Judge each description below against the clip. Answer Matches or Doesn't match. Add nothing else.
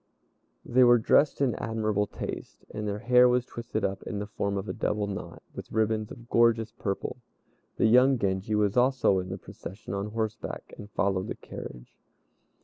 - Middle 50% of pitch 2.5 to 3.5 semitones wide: Matches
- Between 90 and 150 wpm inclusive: Doesn't match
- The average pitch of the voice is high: Doesn't match